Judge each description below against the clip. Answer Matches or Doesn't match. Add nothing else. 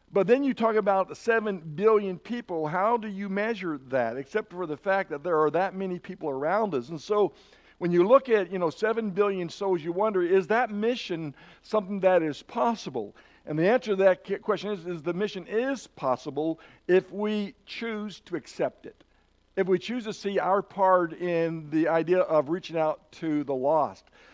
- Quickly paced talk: Doesn't match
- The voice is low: Doesn't match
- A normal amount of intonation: Matches